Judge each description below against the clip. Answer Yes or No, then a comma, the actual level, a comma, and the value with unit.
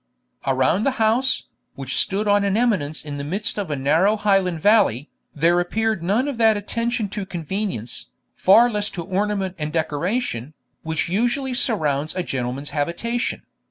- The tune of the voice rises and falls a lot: Yes, wide, 6.2 semitones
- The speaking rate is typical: Yes, average, 160 wpm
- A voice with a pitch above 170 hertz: Yes, high, 190 Hz